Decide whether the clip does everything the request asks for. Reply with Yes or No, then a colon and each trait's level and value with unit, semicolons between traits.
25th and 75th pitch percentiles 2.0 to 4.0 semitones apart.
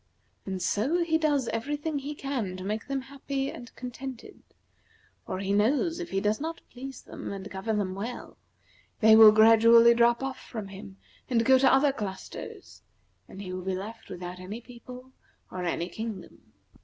No: average, 5.3 semitones